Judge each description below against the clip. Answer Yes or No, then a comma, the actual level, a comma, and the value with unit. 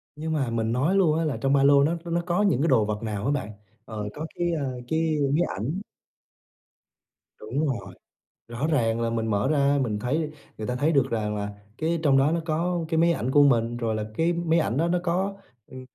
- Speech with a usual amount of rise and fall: No, wide, 5.9 semitones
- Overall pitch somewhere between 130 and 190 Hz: Yes, medium, 140 Hz